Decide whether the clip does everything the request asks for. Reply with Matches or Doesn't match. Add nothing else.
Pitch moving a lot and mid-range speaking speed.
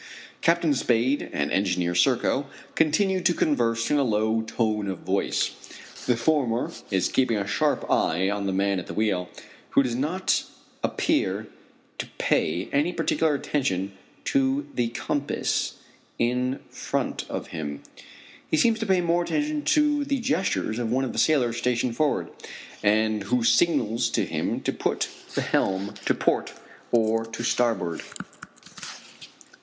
Matches